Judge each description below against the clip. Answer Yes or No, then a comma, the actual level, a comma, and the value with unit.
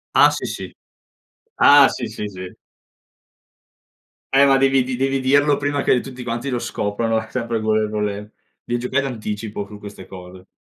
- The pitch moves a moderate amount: Yes, average, 4.4 semitones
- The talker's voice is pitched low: Yes, low, 115 Hz